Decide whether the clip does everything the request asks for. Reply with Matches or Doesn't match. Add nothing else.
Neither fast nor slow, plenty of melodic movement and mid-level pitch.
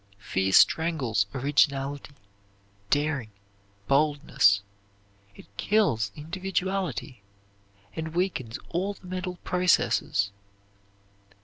Doesn't match